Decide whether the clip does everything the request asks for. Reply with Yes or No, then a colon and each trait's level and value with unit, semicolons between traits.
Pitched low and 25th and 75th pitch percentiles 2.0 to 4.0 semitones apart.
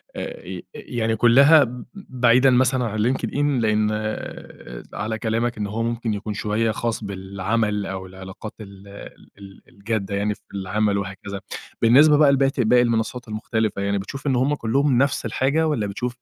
Yes: low, 115 Hz; average, 3.7 semitones